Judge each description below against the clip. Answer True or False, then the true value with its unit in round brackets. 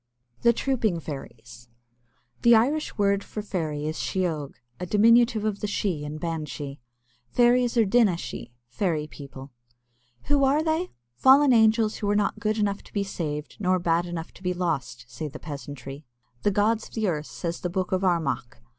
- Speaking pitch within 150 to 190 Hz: True (185 Hz)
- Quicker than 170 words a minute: True (180 wpm)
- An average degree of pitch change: False (6.4 semitones)